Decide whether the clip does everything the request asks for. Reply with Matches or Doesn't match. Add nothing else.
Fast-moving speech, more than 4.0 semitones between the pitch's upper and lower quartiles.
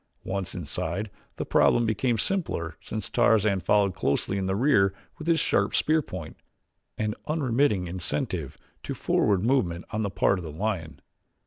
Doesn't match